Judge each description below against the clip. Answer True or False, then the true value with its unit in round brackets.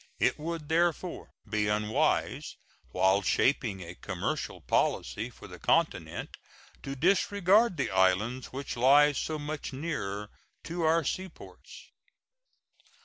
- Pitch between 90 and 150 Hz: True (140 Hz)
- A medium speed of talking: False (115 wpm)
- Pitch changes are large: True (7.9 semitones)